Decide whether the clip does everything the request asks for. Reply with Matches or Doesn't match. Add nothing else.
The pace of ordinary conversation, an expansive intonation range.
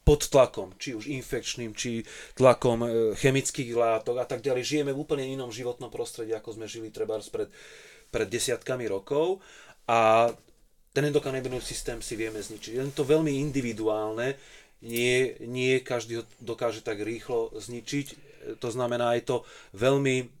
Doesn't match